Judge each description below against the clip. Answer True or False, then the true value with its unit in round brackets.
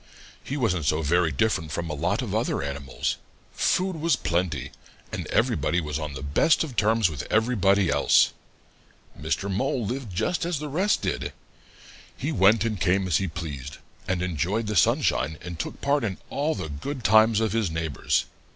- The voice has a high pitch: False (95 Hz)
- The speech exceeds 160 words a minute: True (180 wpm)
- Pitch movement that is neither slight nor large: False (6.1 semitones)